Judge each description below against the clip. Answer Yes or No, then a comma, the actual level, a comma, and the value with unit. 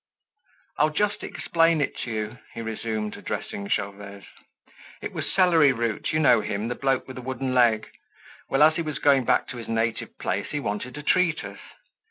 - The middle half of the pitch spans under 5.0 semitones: No, wide, 5.4 semitones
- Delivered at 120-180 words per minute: No, average, 190 wpm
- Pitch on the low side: Yes, low, 125 Hz